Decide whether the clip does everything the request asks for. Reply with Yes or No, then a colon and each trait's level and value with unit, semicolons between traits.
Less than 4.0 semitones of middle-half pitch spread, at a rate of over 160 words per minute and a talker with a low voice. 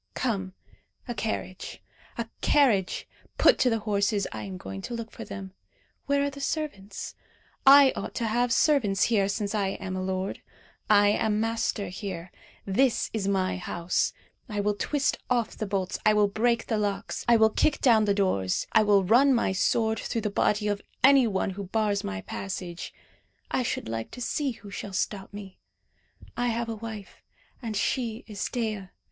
No: average, 3.2 semitones; average, 180 wpm; high, 210 Hz